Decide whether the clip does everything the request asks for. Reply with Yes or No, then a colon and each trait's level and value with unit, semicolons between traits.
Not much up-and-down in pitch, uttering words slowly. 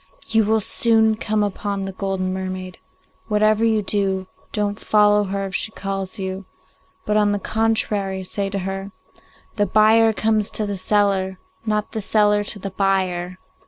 No: narrow, 1.9 semitones; average, 160 wpm